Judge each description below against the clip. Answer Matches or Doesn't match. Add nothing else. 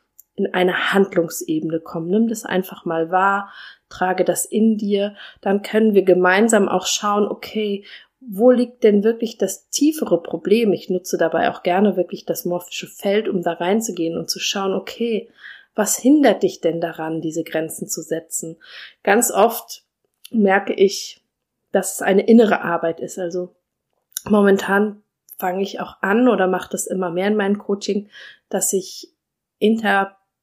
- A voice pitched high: Matches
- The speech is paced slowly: Doesn't match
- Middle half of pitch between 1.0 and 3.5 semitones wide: Matches